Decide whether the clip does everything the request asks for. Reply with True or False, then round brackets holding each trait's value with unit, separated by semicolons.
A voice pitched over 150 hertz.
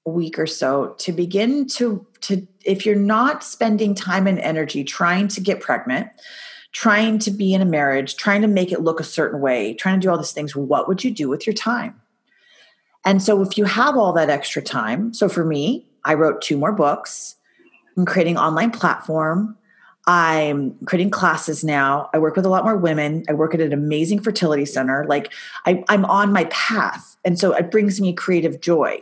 True (185 Hz)